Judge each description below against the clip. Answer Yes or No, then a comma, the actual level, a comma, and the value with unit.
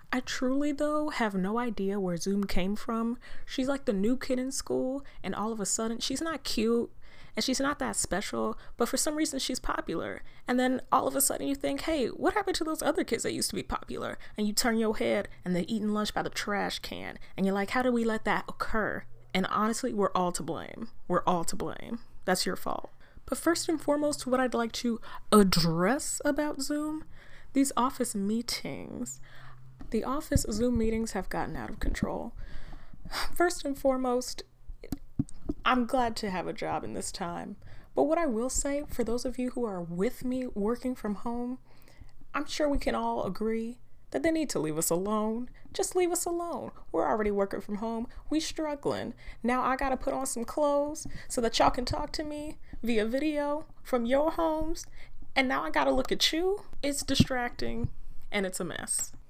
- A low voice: No, high, 245 Hz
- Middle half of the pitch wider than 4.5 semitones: Yes, average, 5.2 semitones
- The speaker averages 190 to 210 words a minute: Yes, average, 200 wpm